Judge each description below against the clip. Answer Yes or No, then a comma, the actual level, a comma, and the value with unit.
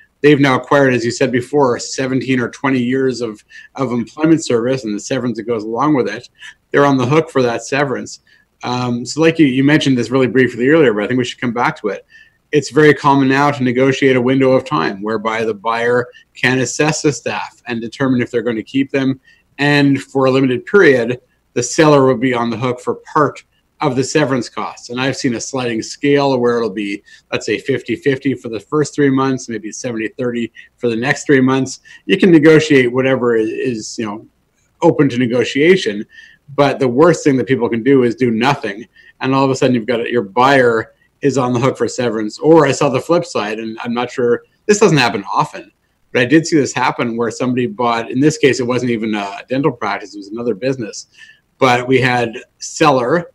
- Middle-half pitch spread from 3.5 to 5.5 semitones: No, average, 3.0 semitones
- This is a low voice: Yes, low, 130 Hz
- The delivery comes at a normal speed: No, fast, 215 wpm